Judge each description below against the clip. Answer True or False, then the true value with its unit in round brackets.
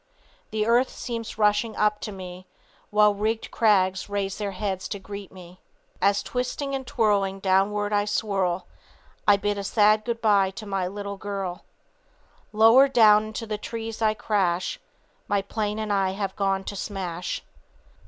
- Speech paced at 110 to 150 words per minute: False (160 wpm)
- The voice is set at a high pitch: True (205 Hz)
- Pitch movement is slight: True (1.9 semitones)